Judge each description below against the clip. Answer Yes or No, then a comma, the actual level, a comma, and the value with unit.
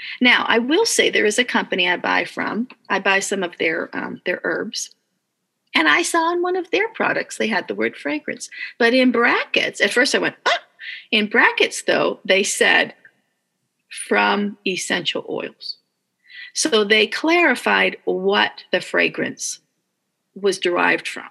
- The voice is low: No, high, 245 Hz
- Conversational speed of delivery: Yes, average, 160 wpm